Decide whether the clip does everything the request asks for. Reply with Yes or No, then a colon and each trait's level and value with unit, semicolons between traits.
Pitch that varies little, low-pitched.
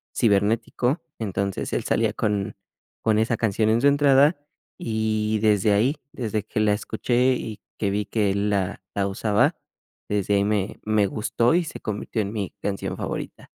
Yes: narrow, 2.1 semitones; low, 105 Hz